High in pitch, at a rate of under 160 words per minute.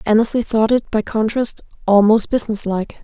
Yes: high, 220 Hz; average, 140 wpm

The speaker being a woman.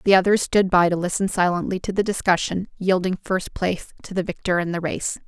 Yes: female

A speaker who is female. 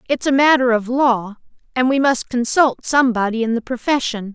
Yes: female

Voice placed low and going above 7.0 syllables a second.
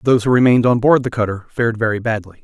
Yes: low, 115 Hz; 7.6 syllables/s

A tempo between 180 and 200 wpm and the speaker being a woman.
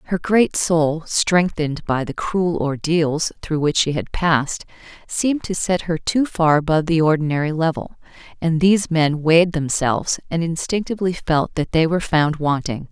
No: average, 165 wpm; female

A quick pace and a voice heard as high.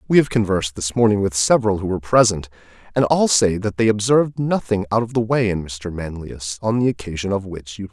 No: fast, 235 wpm; low, 105 Hz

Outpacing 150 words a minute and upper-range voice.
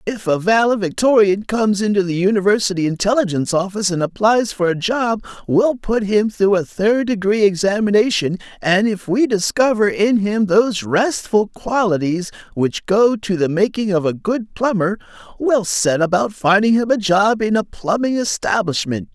Yes: average, 160 wpm; high, 205 Hz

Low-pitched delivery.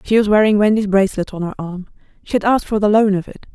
No: high, 205 Hz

